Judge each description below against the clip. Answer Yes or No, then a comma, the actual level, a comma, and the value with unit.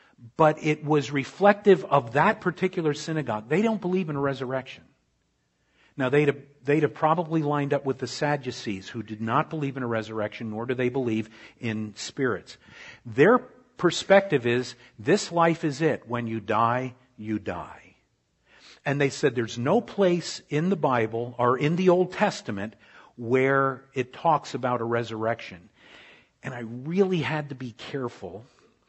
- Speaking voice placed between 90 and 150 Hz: Yes, low, 135 Hz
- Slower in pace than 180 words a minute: Yes, average, 160 wpm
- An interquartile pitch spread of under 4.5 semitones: No, average, 4.9 semitones